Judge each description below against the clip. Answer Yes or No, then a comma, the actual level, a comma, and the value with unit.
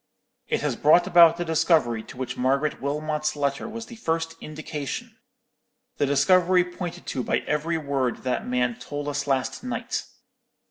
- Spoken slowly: No, average, 150 wpm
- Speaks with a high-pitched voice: No, medium, 150 Hz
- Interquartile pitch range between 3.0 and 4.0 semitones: Yes, average, 3.6 semitones